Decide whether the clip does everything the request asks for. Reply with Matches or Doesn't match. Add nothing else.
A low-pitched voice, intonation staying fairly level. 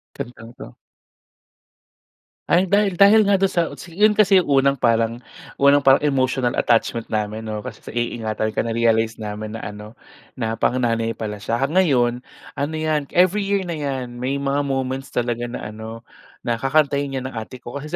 Doesn't match